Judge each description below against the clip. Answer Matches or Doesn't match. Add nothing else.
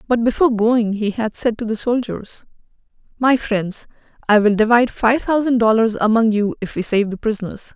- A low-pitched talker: Doesn't match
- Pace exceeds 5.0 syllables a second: Matches